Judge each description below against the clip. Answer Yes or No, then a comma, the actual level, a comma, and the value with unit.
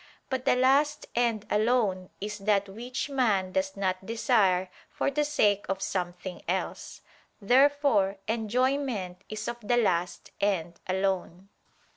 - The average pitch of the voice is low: No, high, 210 Hz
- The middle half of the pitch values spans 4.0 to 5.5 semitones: Yes, average, 4.7 semitones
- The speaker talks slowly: Yes, slow, 130 wpm